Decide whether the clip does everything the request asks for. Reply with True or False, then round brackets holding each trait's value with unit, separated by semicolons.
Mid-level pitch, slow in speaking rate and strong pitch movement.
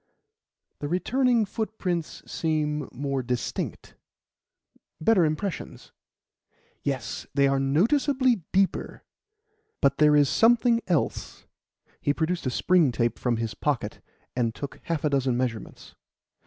True (150 Hz; 115 wpm; 6.3 semitones)